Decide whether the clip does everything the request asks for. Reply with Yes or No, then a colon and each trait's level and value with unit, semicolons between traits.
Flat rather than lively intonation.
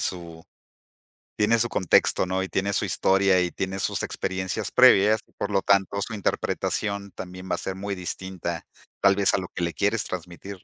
Yes: narrow, 1.6 semitones